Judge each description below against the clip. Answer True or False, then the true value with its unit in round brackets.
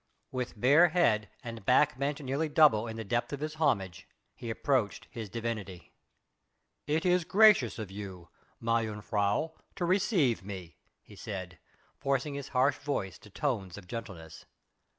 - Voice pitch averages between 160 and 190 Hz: False (115 Hz)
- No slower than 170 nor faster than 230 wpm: False (150 wpm)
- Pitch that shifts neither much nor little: False (6.0 semitones)